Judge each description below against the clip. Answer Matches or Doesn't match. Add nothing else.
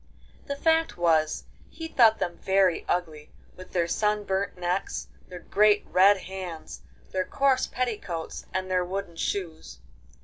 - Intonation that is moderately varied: Matches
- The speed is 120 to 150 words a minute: Matches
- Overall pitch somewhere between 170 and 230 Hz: Matches